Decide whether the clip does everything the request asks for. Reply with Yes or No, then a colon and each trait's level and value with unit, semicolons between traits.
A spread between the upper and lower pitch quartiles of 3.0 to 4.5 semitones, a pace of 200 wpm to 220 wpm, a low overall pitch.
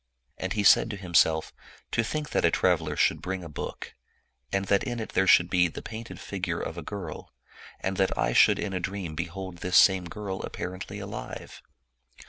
No: narrow, 2.5 semitones; fast, 205 wpm; very low, 95 Hz